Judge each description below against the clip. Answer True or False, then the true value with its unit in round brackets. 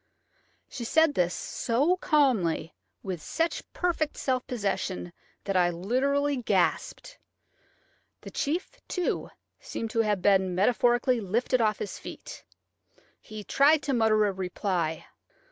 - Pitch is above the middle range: True (225 Hz)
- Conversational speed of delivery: False (125 wpm)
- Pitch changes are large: True (6.7 semitones)